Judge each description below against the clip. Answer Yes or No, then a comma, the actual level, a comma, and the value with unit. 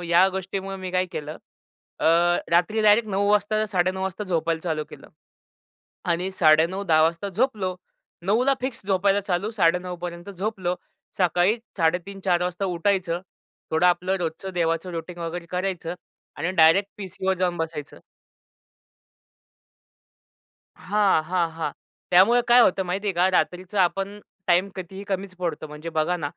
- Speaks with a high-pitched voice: No, medium, 180 Hz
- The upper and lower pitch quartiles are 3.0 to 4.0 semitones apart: No, narrow, 2.5 semitones